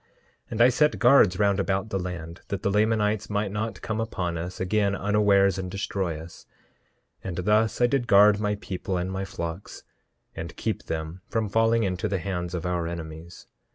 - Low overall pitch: Yes, low, 100 Hz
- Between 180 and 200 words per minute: Yes, average, 190 wpm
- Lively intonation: No, average, 3.0 semitones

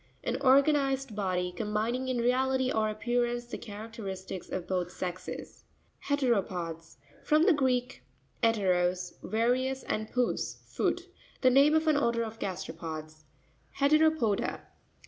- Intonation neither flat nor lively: No, wide, 6.0 semitones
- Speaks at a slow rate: Yes, slow, 125 wpm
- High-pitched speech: Yes, high, 230 Hz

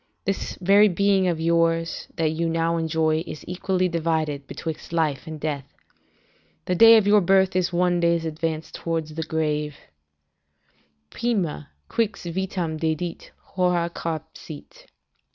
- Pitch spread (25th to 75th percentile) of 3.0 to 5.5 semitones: No, narrow, 2.4 semitones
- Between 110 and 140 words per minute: Yes, slow, 135 wpm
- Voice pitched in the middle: Yes, medium, 165 Hz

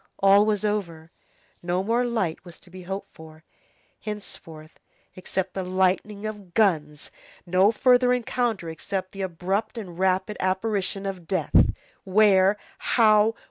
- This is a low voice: No, high, 190 Hz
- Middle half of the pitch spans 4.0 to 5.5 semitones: No, average, 2.8 semitones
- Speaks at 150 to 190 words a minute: No, slow, 135 wpm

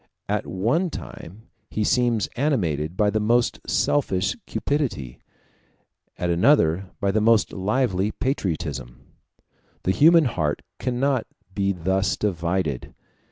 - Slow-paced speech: Yes, slow, 115 wpm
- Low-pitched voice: Yes, low, 100 Hz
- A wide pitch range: Yes, wide, 5.9 semitones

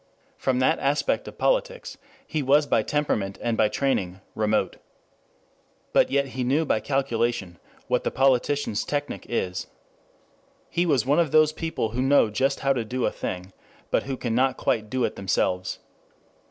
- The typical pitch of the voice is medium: No, low, 130 Hz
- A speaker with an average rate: Yes, average, 165 wpm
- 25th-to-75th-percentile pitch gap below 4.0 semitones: No, average, 4.8 semitones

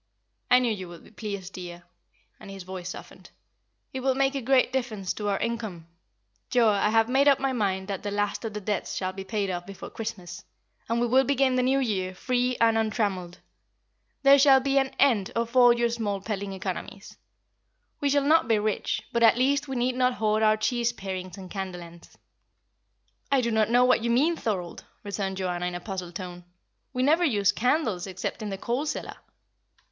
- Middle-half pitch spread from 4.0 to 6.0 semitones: Yes, average, 4.7 semitones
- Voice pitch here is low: No, high, 220 Hz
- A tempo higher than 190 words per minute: Yes, fast, 205 wpm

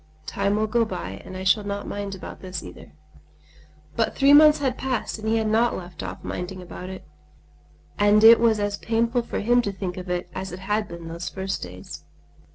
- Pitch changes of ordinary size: Yes, average, 3.6 semitones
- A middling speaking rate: No, fast, 210 wpm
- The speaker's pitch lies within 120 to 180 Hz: No, high, 205 Hz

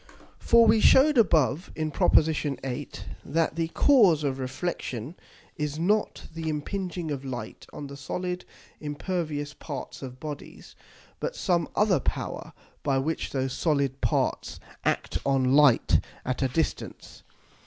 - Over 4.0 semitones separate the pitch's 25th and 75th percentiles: Yes, average, 4.5 semitones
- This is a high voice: No, medium, 150 Hz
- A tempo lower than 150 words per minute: Yes, average, 140 wpm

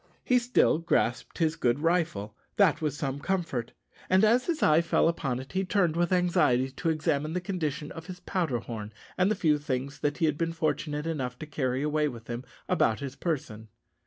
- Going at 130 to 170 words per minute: No, fast, 205 wpm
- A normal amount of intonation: Yes, average, 4.6 semitones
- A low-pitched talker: No, medium, 155 Hz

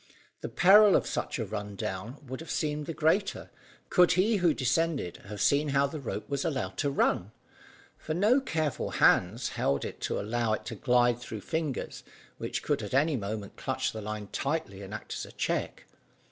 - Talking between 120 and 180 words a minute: No, average, 190 wpm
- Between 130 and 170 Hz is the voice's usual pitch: Yes, low, 135 Hz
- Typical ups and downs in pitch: No, wide, 7.0 semitones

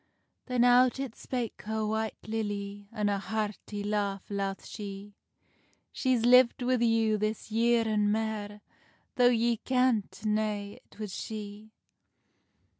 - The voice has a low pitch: No, high, 215 Hz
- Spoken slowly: Yes, slow, 125 wpm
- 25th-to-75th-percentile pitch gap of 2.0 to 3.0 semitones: Yes, narrow, 2.4 semitones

